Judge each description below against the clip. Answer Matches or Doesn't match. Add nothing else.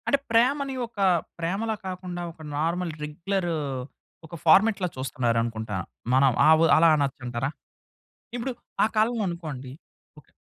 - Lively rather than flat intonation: Matches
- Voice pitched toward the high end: Doesn't match